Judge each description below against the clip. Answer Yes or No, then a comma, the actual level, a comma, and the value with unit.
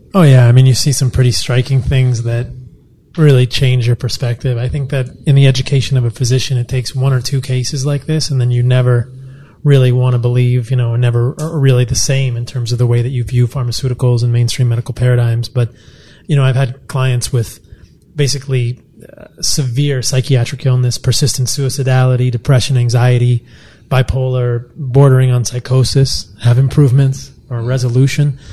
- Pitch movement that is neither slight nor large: No, narrow, 1.7 semitones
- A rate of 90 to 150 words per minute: No, average, 175 wpm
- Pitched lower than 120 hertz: No, low, 125 Hz